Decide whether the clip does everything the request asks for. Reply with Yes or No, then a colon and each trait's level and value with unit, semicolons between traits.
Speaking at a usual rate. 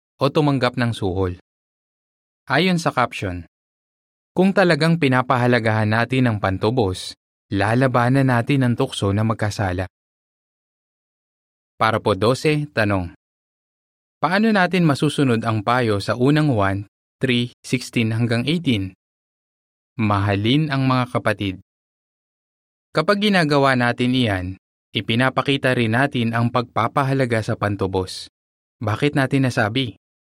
No: slow, 105 wpm